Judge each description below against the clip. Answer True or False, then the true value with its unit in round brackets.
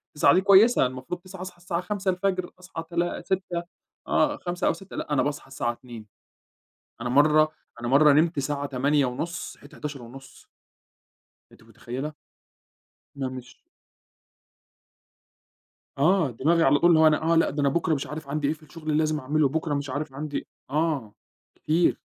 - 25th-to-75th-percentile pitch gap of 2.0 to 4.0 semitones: True (3.7 semitones)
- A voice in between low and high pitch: True (150 Hz)